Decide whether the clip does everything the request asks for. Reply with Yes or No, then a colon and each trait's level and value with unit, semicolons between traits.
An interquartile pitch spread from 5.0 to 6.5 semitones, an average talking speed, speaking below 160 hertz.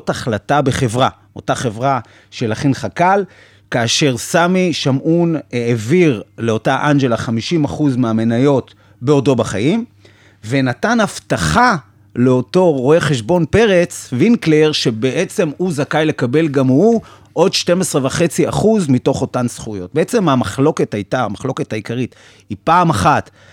Yes: average, 5.3 semitones; average, 110 wpm; low, 135 Hz